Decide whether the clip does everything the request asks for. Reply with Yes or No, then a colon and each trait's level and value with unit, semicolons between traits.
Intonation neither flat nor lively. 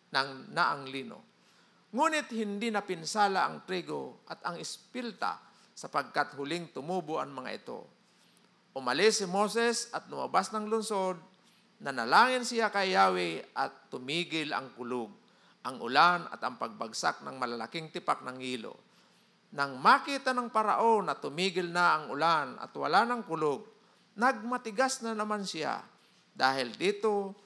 No: wide, 7.1 semitones